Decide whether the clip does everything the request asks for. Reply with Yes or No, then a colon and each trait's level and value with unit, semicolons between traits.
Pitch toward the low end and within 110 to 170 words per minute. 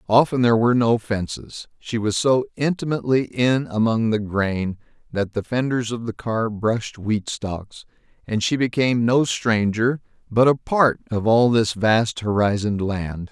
Yes: low, 115 Hz; average, 160 wpm